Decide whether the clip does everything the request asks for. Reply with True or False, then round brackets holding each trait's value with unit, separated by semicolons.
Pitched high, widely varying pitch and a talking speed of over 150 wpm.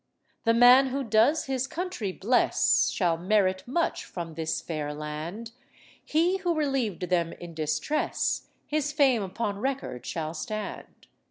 False (215 Hz; 8.1 semitones; 140 wpm)